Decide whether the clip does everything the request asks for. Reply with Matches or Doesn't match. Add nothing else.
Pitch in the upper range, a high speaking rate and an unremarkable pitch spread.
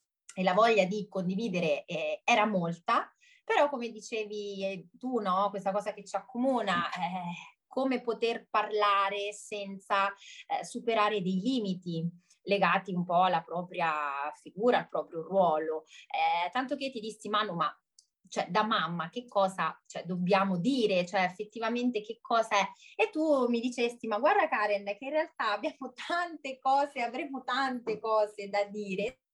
Doesn't match